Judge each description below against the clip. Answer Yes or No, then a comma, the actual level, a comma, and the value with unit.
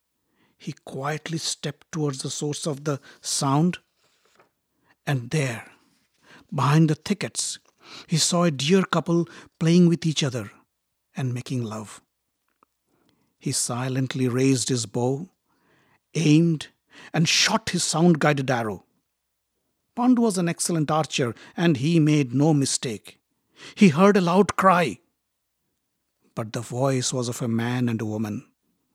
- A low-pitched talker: No, medium, 150 Hz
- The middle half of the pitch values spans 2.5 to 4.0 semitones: No, average, 4.5 semitones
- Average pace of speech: No, slow, 130 wpm